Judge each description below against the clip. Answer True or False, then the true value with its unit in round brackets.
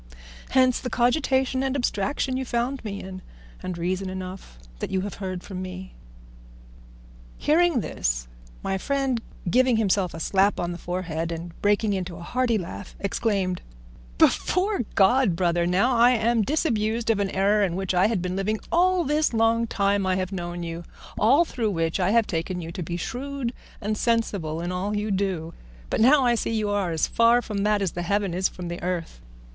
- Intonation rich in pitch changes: False (4.7 semitones)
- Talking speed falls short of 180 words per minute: False (190 wpm)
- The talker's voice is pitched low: False (200 Hz)